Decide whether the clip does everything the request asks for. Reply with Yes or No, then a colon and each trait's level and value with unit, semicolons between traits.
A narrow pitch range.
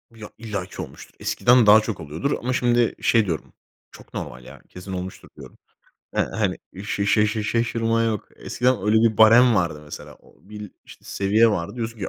No: average, 3.5 semitones